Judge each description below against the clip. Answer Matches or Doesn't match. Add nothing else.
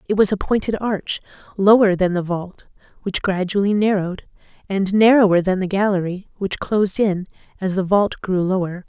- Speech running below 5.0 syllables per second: Doesn't match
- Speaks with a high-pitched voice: Matches